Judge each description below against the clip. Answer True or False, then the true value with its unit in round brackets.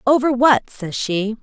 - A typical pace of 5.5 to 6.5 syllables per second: False (4.0 syllables/s)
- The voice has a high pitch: True (240 Hz)